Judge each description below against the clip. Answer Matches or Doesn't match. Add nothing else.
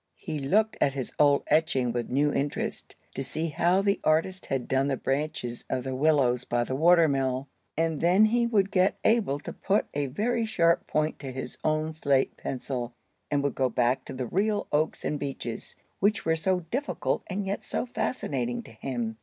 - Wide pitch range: Matches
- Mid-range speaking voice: Matches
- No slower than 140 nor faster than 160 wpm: Doesn't match